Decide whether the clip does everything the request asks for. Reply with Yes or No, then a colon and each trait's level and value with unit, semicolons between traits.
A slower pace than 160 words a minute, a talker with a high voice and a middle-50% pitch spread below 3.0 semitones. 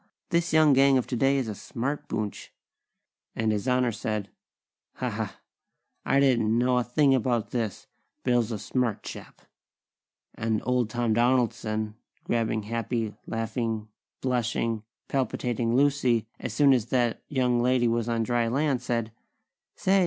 No: average, 145 wpm; low, 120 Hz; narrow, 2.4 semitones